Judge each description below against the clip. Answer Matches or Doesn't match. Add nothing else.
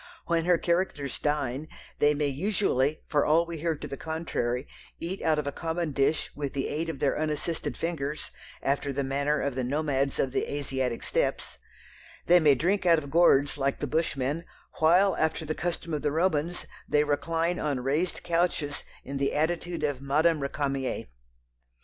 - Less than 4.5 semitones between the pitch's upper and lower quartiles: Matches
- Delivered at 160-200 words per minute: Matches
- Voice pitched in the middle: Matches